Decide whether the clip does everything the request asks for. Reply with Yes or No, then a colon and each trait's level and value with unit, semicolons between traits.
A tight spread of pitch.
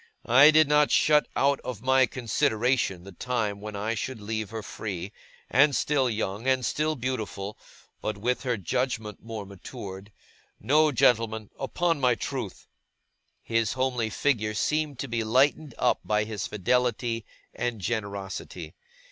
No: average, 3.8 semitones